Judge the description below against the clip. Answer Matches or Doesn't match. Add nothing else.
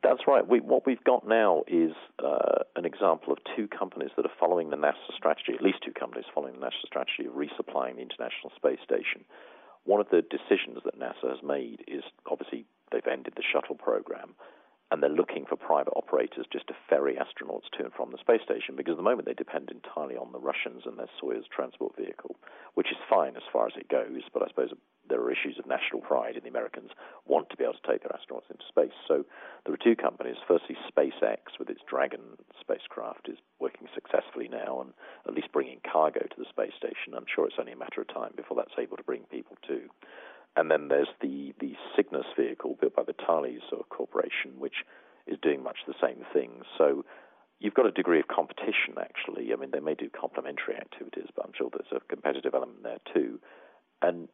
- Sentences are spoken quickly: Matches